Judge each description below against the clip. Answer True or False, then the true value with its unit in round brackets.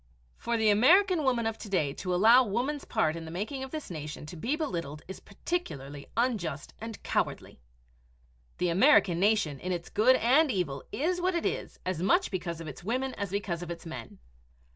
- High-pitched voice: True (200 Hz)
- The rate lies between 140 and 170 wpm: False (195 wpm)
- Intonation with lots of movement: True (7.4 semitones)